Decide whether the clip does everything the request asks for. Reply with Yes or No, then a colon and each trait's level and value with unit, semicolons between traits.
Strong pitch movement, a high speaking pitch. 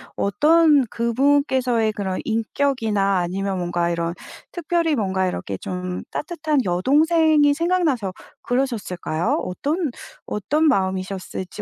Yes: wide, 7.9 semitones; high, 230 Hz